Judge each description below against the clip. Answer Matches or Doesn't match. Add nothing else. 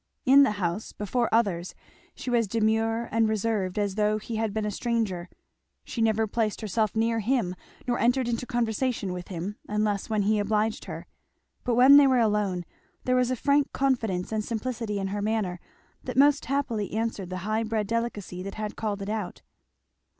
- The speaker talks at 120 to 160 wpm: Doesn't match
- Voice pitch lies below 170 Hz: Doesn't match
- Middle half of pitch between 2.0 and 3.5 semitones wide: Matches